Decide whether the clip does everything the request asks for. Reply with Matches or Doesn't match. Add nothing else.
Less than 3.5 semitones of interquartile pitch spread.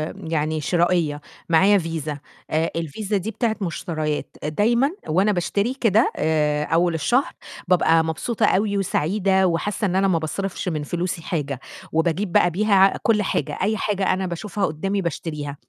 Doesn't match